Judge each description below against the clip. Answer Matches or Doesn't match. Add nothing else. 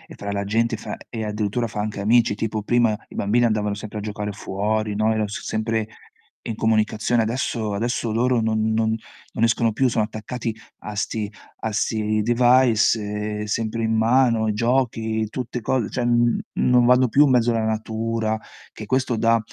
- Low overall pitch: Matches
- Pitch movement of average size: Doesn't match